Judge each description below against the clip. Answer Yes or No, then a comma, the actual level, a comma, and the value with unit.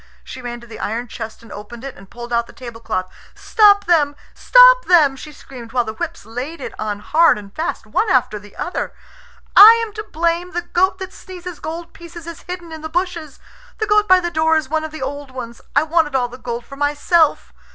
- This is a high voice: Yes, very high, 310 Hz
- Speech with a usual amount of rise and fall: No, wide, 6.4 semitones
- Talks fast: Yes, fast, 225 wpm